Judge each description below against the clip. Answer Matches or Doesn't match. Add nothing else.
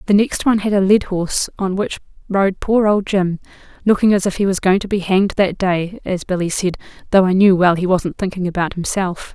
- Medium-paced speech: Doesn't match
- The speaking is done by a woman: Matches